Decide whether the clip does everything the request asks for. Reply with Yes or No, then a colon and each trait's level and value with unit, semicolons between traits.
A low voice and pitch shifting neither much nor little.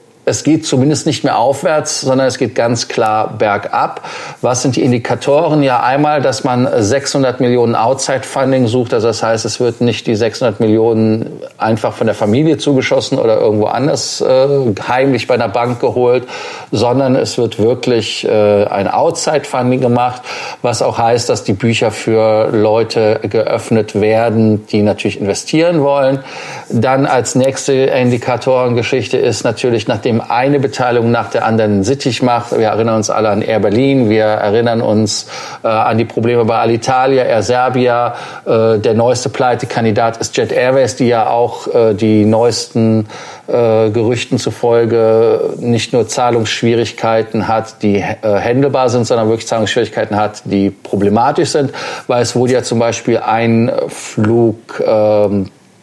Yes: low, 120 Hz; average, 3.0 semitones